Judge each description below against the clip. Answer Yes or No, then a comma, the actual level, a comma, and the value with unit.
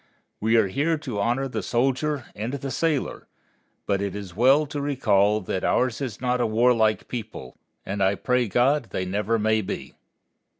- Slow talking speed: No, average, 175 wpm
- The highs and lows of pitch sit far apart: No, average, 4.4 semitones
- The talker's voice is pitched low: Yes, low, 115 Hz